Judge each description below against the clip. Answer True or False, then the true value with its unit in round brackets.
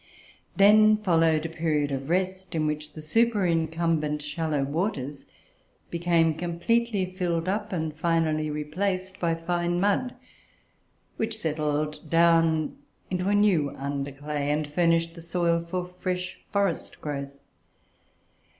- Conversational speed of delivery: False (125 wpm)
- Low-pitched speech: False (165 Hz)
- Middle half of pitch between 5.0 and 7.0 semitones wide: False (3.3 semitones)